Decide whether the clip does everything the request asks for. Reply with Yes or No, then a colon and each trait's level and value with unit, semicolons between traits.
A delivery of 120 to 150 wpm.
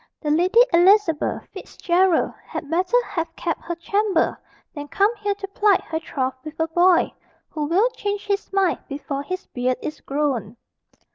No: average, 160 wpm